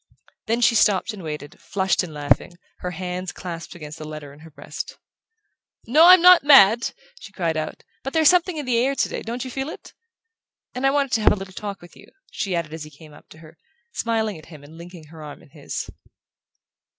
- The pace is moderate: No, fast, 220 wpm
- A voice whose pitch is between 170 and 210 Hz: Yes, medium, 185 Hz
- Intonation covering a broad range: Yes, wide, 7.3 semitones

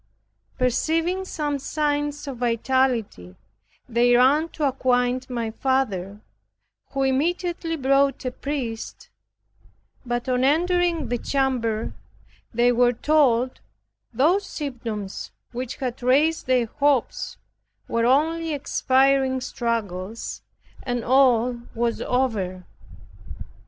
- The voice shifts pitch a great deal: No, average, 3.4 semitones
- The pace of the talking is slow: Yes, slow, 100 wpm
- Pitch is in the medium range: No, very high, 255 Hz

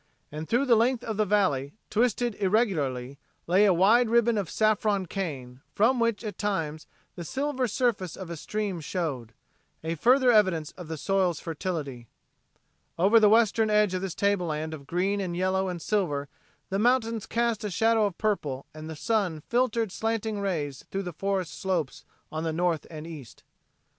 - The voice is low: No, high, 190 Hz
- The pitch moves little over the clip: No, wide, 5.4 semitones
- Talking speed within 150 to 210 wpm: Yes, average, 175 wpm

